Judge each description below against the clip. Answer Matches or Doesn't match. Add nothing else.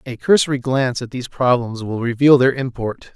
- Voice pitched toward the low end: Matches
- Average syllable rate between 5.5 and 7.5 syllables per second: Matches